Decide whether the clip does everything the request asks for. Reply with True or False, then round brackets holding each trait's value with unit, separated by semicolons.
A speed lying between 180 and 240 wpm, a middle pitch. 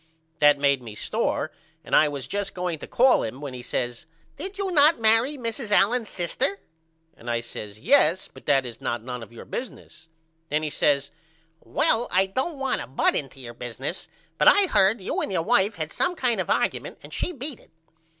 True (205 wpm; 175 Hz)